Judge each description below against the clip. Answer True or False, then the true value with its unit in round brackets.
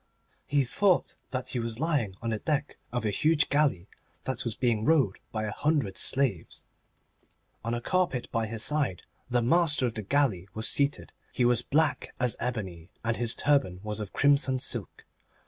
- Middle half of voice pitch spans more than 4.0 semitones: True (4.7 semitones)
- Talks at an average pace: True (180 wpm)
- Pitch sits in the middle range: False (125 Hz)